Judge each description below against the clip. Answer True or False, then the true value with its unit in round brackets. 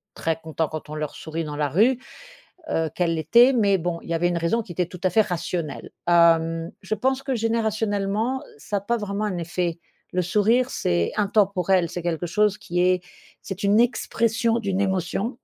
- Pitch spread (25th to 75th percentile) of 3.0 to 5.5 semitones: True (4.4 semitones)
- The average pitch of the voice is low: False (185 Hz)